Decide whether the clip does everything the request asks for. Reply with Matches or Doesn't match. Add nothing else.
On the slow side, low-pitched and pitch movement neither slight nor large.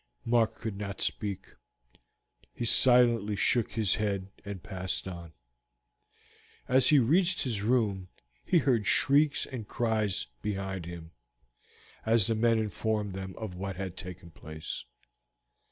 Matches